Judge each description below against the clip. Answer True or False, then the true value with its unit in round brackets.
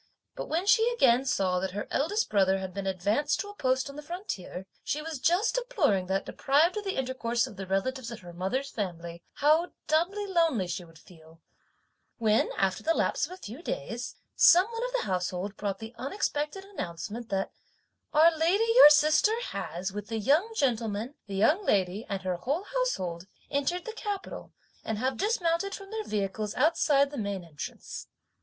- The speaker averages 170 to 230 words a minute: True (185 wpm)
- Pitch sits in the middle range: False (260 Hz)